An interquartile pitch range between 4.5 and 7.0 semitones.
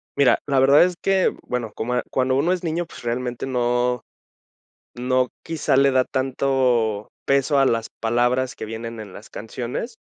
No: narrow, 2.5 semitones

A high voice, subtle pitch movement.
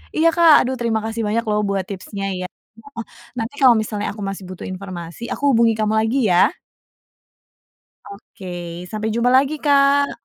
No: high, 220 Hz; average, 3.9 semitones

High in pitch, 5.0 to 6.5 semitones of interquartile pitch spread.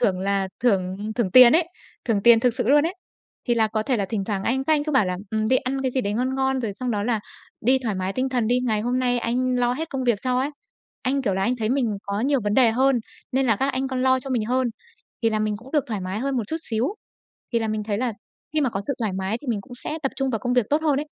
No: high, 245 Hz; average, 3.6 semitones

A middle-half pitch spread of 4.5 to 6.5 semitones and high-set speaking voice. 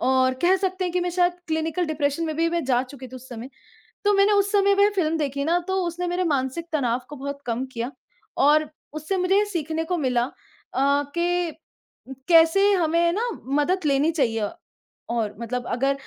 Yes: average, 5.1 semitones; very high, 315 Hz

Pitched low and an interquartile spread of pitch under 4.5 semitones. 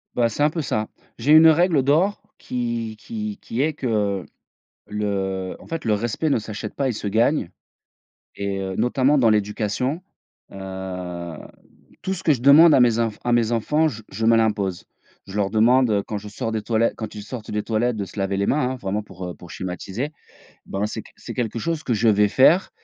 No: low, 110 Hz; average, 4.8 semitones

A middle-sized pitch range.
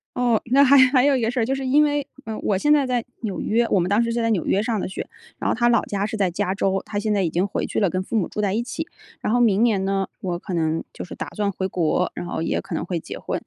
Yes: average, 4.0 semitones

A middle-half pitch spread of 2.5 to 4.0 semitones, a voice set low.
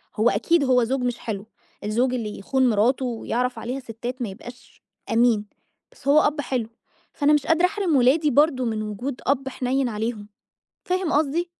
No: average, 3.7 semitones; very high, 255 Hz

